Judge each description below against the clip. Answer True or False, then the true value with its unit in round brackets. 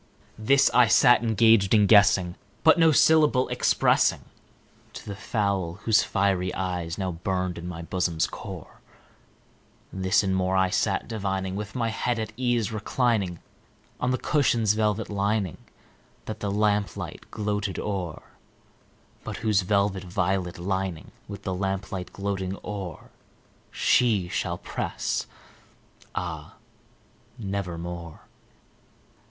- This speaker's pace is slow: True (120 wpm)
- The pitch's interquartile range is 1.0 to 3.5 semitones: True (2.9 semitones)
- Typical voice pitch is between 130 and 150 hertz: False (100 Hz)